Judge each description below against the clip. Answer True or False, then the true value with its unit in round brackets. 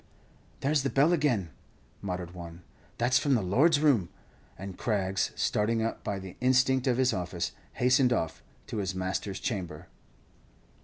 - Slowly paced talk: False (150 wpm)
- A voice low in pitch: True (105 Hz)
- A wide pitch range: True (6.0 semitones)